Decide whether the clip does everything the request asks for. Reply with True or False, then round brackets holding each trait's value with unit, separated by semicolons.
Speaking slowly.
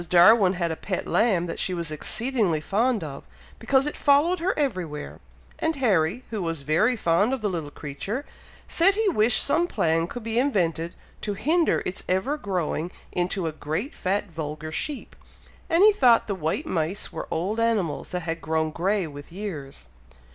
False (175 wpm)